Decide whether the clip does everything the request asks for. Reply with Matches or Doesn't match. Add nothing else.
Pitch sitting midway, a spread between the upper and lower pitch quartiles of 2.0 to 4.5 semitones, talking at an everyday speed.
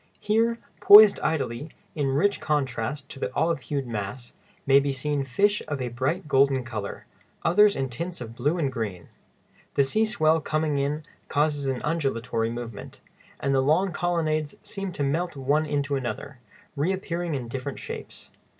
Matches